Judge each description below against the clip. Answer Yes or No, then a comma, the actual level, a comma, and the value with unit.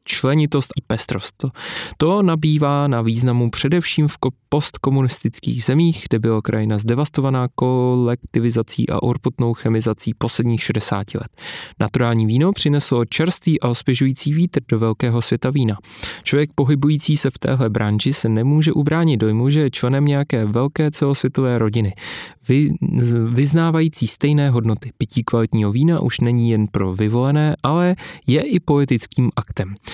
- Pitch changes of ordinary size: Yes, average, 4.3 semitones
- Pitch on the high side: No, low, 130 Hz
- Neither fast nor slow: Yes, average, 135 wpm